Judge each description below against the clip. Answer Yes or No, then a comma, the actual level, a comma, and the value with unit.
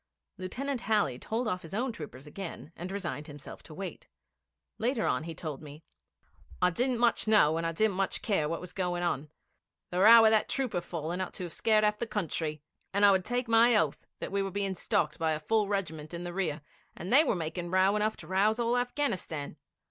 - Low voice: No, high, 190 Hz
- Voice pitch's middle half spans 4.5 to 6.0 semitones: Yes, average, 5.0 semitones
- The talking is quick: Yes, fast, 215 wpm